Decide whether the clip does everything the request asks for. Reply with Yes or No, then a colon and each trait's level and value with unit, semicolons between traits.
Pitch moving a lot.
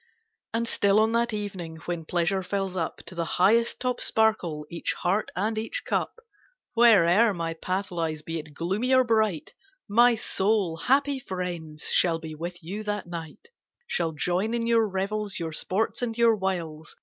No: average, 4.9 semitones